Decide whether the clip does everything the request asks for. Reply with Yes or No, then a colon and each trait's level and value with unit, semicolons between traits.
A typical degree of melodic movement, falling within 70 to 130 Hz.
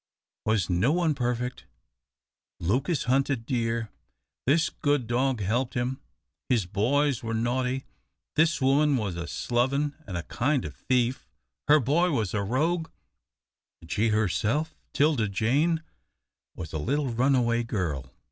Yes: average, 4.6 semitones; low, 125 Hz